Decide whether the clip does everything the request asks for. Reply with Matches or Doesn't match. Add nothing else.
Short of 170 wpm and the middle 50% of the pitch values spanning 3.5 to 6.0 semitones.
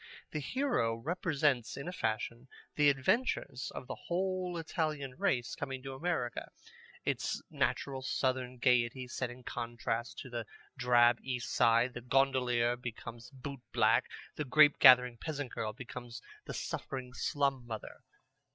Doesn't match